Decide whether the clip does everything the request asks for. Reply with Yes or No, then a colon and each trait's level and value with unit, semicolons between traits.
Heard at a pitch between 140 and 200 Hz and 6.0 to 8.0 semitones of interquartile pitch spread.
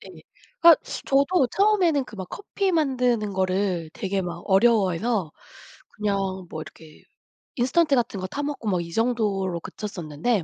No: high, 210 Hz; wide, 6.6 semitones